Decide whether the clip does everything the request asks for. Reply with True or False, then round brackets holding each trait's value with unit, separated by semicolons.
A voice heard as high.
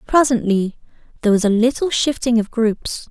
True (235 Hz)